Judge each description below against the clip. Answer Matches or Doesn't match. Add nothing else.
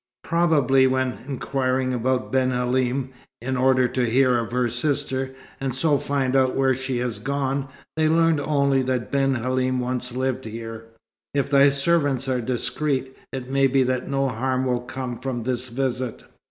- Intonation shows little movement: Matches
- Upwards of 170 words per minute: Doesn't match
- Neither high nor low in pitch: Doesn't match